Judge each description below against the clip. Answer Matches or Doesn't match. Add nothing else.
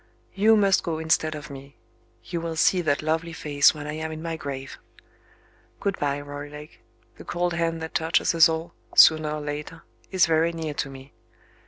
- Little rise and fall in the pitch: Matches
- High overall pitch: Doesn't match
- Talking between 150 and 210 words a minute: Matches